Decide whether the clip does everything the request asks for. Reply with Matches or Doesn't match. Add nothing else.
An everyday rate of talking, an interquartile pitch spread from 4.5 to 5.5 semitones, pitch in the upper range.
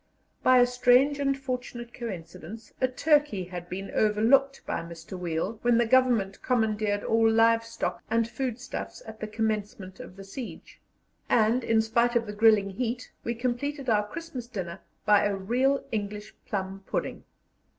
Doesn't match